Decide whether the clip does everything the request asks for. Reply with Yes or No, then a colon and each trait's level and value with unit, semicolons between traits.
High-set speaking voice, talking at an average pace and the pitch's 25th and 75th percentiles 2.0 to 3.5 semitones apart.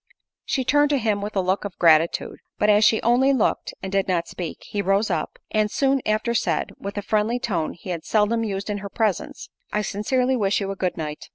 No: high, 205 Hz; fast, 225 wpm; average, 2.9 semitones